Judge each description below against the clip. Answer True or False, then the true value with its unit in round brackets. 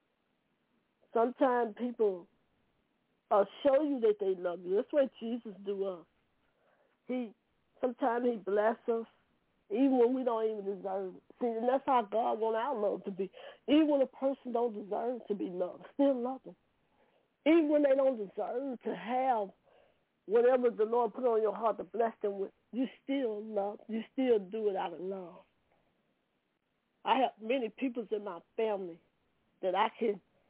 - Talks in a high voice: True (230 Hz)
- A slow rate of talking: False (170 wpm)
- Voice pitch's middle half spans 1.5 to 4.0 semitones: True (3.7 semitones)